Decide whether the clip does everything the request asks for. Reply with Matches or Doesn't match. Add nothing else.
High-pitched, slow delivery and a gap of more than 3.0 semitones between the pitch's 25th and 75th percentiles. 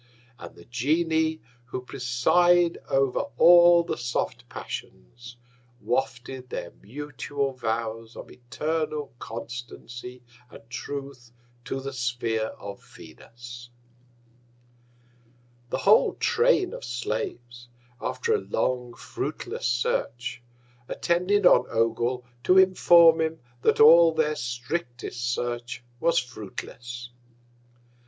Doesn't match